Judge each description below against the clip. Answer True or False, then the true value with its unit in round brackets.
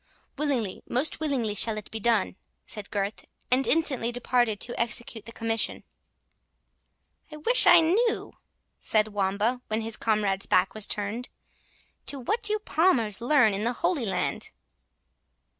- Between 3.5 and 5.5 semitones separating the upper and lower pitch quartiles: True (5.0 semitones)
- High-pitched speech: True (235 Hz)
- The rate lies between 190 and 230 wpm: False (140 wpm)